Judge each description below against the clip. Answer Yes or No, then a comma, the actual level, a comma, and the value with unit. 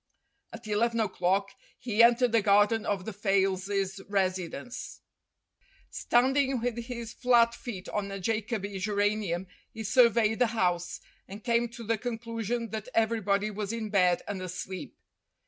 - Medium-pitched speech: No, high, 215 Hz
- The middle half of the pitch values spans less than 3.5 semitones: Yes, average, 2.9 semitones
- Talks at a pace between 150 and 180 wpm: No, average, 140 wpm